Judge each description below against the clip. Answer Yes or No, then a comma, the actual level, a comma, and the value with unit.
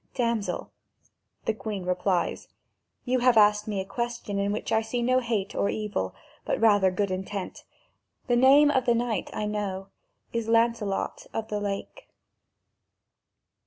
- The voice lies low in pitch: No, high, 215 Hz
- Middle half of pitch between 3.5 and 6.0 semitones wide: No, average, 3.0 semitones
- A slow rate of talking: No, average, 150 wpm